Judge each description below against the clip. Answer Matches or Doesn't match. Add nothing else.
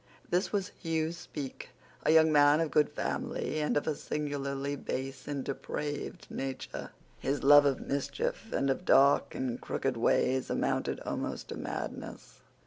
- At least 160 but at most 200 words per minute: Doesn't match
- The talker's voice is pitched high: Doesn't match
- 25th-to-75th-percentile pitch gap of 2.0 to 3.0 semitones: Matches